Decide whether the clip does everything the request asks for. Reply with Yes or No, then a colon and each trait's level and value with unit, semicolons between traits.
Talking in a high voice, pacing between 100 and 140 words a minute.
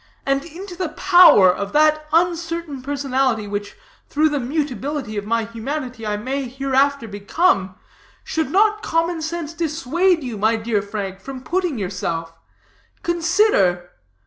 Yes: very high, 275 Hz; slow, 135 wpm